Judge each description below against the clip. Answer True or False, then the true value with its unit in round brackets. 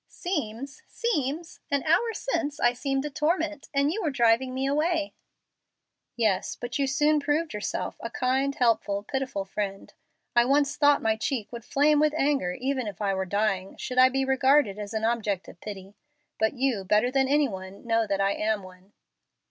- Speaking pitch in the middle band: False (255 Hz)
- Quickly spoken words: False (185 wpm)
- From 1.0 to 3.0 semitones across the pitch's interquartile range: False (5.4 semitones)